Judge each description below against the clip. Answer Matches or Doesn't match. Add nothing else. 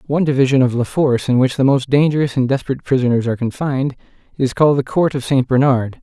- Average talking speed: Doesn't match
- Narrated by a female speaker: Doesn't match